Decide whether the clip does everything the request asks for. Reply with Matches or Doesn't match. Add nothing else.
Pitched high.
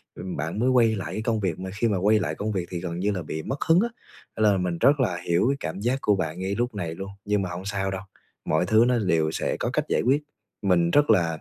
Doesn't match